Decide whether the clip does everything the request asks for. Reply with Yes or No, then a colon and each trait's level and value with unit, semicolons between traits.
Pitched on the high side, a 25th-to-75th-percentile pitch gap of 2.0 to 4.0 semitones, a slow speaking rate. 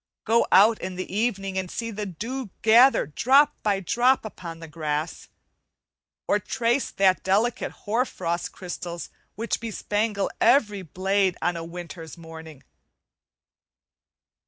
No: high, 195 Hz; average, 4.7 semitones; slow, 130 wpm